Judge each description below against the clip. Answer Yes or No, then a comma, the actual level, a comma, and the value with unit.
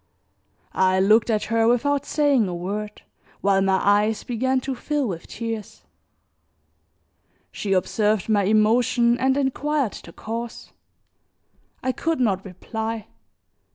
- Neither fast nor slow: No, slow, 120 wpm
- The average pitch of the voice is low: No, high, 220 Hz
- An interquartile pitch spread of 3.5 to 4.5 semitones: Yes, average, 3.9 semitones